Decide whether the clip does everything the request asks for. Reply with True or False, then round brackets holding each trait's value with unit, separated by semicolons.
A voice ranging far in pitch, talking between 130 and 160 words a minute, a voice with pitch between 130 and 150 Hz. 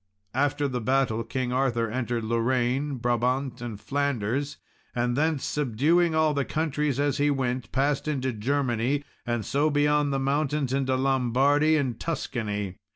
False (3.0 semitones; 145 wpm; 135 Hz)